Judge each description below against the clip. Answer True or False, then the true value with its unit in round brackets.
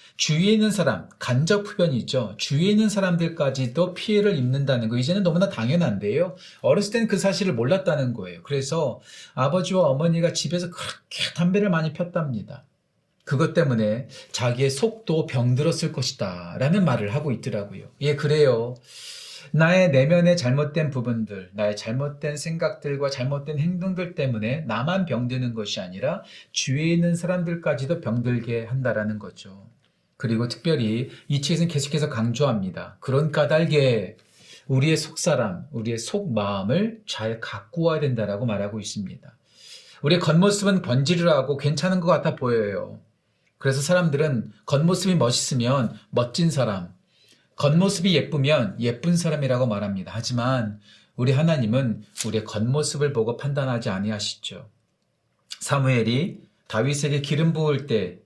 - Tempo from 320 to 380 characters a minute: True (340 characters per minute)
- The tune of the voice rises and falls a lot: True (6.2 semitones)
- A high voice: False (145 Hz)